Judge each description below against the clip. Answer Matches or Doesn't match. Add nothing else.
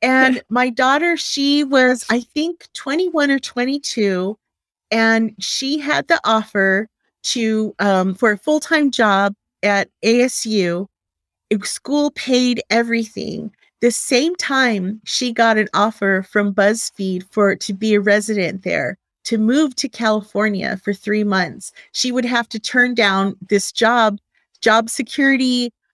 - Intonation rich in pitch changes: Doesn't match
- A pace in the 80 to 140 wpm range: Matches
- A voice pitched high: Matches